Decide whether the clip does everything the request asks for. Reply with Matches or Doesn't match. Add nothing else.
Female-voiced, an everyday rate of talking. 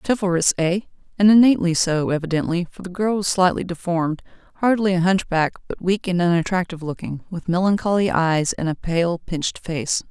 Matches